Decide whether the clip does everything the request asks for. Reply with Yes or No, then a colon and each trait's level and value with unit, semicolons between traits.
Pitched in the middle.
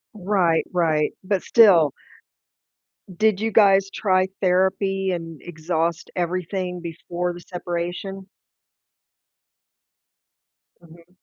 Yes: medium, 180 Hz